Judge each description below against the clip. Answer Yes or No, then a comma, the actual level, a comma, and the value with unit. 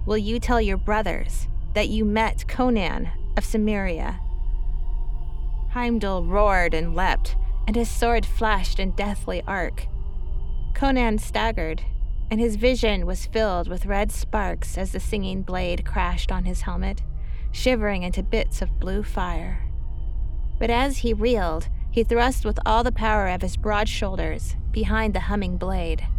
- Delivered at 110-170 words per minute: Yes, average, 145 wpm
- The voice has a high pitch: Yes, high, 200 Hz